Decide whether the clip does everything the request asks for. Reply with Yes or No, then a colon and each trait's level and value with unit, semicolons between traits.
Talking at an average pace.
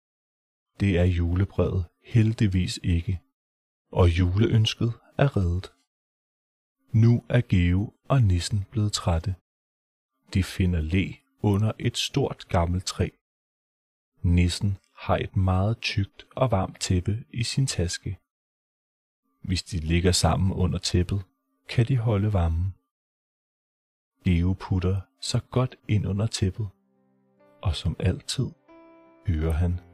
No: slow, 115 wpm